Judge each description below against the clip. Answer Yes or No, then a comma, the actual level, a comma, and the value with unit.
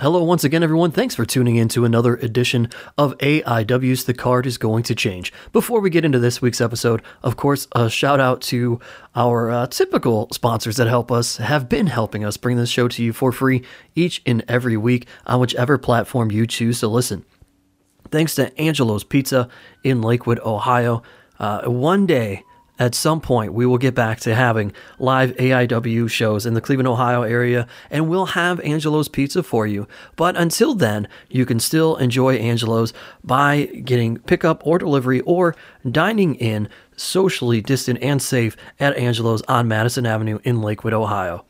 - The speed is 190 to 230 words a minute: No, average, 180 wpm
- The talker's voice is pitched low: Yes, low, 125 Hz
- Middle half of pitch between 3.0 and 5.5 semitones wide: Yes, average, 3.4 semitones